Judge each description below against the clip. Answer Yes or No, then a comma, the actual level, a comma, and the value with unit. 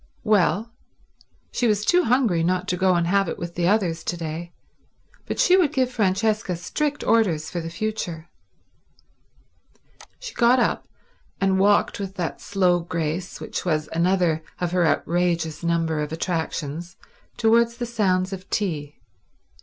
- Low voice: No, medium, 180 Hz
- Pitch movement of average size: Yes, average, 4.2 semitones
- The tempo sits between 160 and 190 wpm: No, average, 150 wpm